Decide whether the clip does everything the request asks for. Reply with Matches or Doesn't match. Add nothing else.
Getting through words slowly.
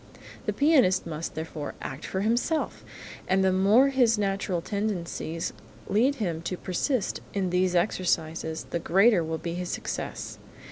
Doesn't match